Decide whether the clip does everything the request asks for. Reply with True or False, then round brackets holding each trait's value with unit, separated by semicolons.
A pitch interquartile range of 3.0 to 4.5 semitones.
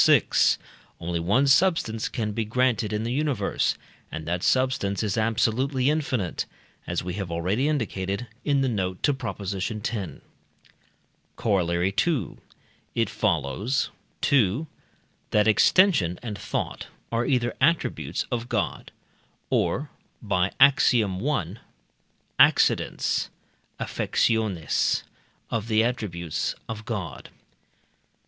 False (5.3 semitones)